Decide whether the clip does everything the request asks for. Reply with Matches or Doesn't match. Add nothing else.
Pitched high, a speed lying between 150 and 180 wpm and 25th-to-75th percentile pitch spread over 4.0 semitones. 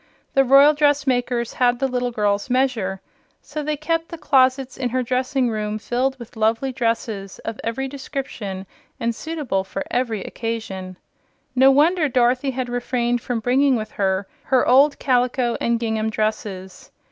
Doesn't match